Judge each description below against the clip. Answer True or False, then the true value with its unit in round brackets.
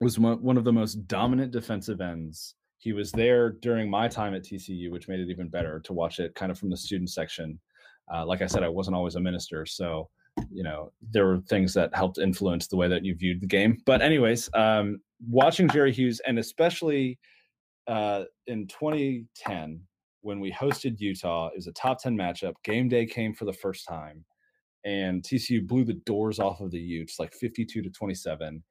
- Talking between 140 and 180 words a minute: False (200 wpm)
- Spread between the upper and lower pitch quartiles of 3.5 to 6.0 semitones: True (4.6 semitones)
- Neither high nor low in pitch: False (100 Hz)